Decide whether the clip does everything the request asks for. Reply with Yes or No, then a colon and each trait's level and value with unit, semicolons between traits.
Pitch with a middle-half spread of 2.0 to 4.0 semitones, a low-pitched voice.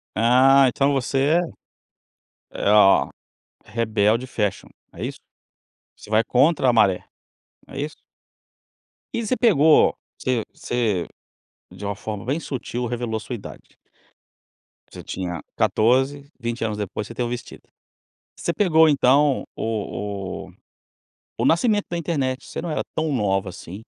No: average, 5.1 semitones; low, 125 Hz